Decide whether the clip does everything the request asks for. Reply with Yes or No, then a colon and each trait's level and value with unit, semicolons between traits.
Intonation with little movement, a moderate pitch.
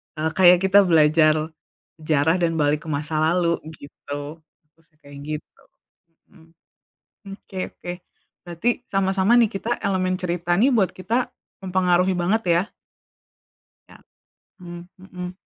No: average, 3.3 semitones; medium, 175 Hz